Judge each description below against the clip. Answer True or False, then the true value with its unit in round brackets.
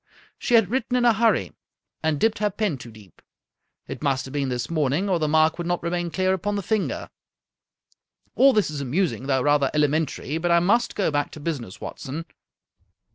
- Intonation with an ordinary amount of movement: False (5.8 semitones)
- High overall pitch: False (160 Hz)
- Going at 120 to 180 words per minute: False (195 wpm)